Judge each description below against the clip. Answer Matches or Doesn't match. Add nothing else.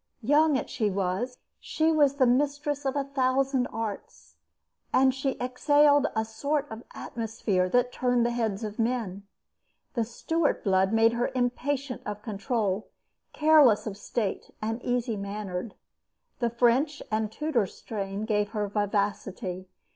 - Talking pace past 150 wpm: Doesn't match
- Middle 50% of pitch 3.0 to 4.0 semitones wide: Doesn't match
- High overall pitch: Matches